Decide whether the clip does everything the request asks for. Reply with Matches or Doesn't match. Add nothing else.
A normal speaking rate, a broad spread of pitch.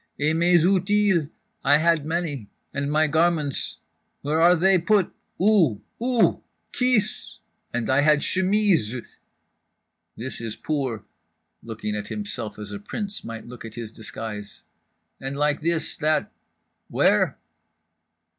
Doesn't match